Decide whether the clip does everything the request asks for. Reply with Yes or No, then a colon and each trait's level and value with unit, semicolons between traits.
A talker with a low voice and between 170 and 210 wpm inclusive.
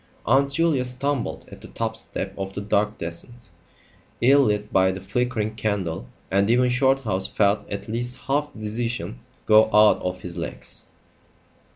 No: low, 110 Hz; average, 160 wpm